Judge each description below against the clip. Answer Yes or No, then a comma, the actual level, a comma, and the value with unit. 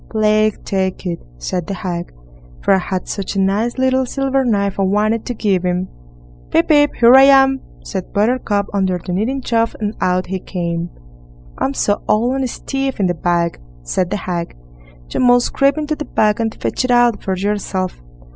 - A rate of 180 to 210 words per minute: Yes, average, 190 wpm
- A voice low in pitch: No, high, 205 Hz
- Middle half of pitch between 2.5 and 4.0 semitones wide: No, average, 4.9 semitones